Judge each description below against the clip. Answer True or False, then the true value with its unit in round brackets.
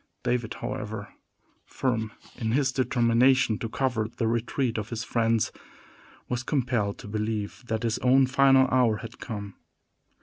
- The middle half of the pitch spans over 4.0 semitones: False (2.7 semitones)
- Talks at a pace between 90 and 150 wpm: True (140 wpm)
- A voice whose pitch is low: True (115 Hz)